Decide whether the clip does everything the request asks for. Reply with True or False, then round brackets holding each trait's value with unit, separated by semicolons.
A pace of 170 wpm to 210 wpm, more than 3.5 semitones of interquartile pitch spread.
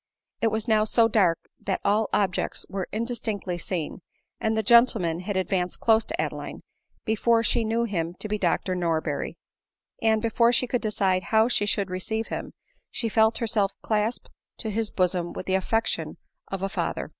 False (180 wpm; 3.2 semitones)